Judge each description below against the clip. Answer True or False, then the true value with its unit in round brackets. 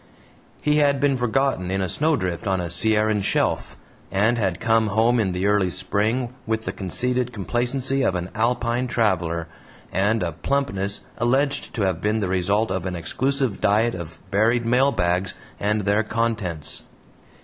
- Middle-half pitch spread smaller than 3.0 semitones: False (4.5 semitones)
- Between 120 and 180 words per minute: True (160 wpm)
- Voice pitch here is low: True (110 Hz)